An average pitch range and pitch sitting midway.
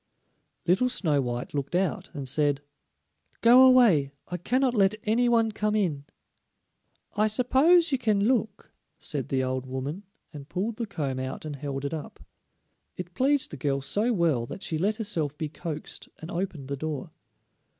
No: wide, 7.5 semitones; medium, 175 Hz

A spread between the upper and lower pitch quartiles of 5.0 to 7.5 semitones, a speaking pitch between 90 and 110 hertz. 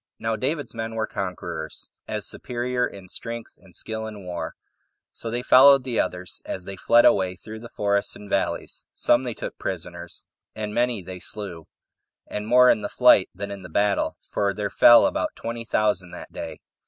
No: average, 3.7 semitones; low, 105 Hz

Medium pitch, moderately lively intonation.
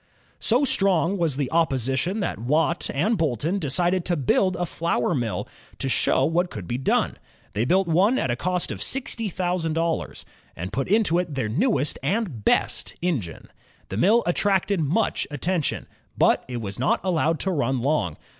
No: medium, 165 Hz; wide, 5.8 semitones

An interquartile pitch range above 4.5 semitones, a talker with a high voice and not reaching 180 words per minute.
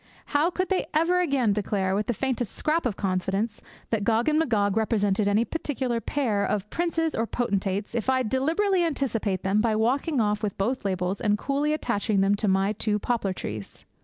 No: wide, 5.4 semitones; high, 225 Hz; average, 190 wpm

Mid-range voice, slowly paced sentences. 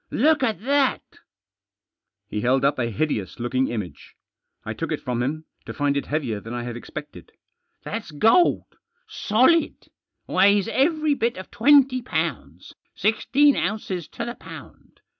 No: medium, 180 Hz; average, 155 wpm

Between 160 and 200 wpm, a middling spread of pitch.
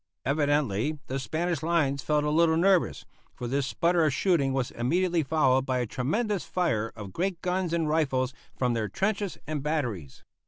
Yes: average, 170 wpm; average, 4.7 semitones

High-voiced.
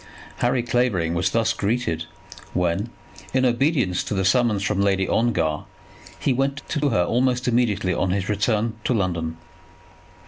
No: low, 105 Hz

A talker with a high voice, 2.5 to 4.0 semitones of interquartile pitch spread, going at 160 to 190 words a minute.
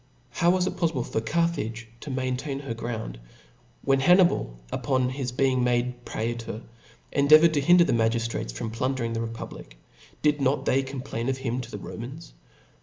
No: low, 130 Hz; average, 3.5 semitones; average, 180 wpm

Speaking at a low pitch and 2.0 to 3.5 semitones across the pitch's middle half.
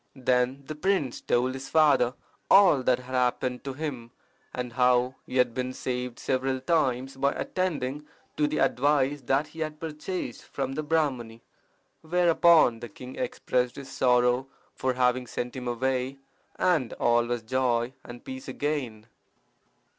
Yes: low, 130 Hz; average, 3.1 semitones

